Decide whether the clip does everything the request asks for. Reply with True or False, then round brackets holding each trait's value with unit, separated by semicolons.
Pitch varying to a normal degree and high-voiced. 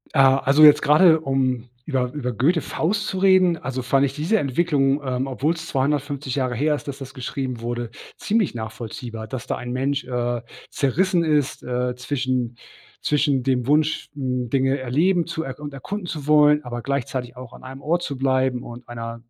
False (3.2 semitones; 135 Hz)